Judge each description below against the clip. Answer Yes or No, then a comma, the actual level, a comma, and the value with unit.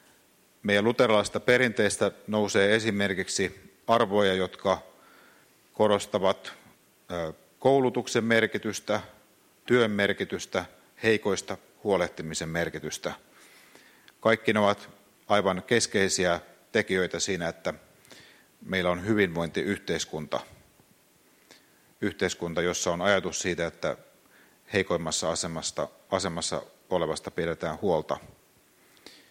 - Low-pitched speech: Yes, low, 100 Hz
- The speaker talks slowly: Yes, slow, 80 wpm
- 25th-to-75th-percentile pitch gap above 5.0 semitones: No, average, 3.6 semitones